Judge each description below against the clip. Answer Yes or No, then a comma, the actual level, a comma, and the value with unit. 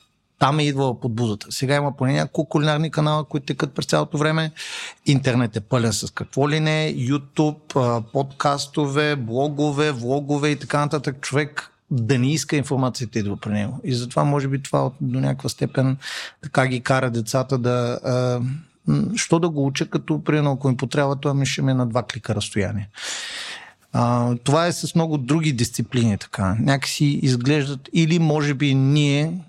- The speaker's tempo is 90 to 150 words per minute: No, fast, 165 wpm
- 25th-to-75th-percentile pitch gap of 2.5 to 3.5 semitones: Yes, average, 3.2 semitones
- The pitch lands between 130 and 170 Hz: Yes, medium, 140 Hz